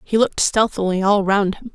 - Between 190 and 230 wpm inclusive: Yes, fast, 205 wpm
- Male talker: No, female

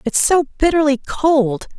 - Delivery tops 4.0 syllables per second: No, 3.7 syllables/s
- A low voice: No, very high, 285 Hz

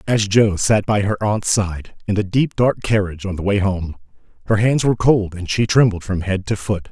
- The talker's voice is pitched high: No, low, 100 Hz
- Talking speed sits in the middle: No, fast, 235 wpm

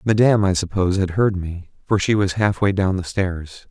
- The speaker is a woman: No, male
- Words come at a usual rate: No, fast, 210 wpm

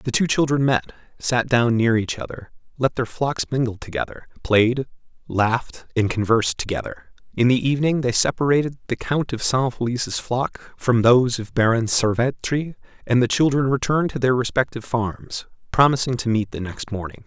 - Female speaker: No, male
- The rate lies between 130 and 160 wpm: No, average, 170 wpm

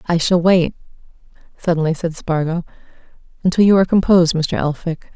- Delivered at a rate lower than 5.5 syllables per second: No, 6.0 syllables/s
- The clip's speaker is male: No, female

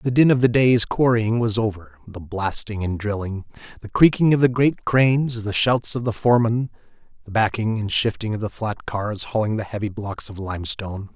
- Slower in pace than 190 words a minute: No, average, 195 wpm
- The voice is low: Yes, low, 110 Hz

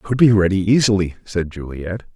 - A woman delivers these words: No, male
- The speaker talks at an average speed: Yes, average, 195 wpm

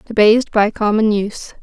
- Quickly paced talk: No, average, 150 wpm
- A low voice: No, high, 215 Hz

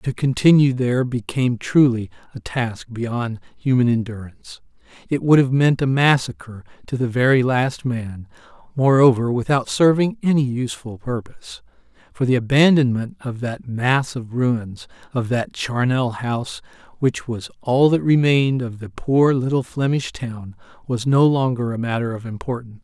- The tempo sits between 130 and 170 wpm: Yes, average, 150 wpm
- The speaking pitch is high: No, low, 125 Hz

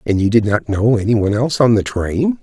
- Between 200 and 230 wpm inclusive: No, fast, 270 wpm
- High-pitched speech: No, low, 110 Hz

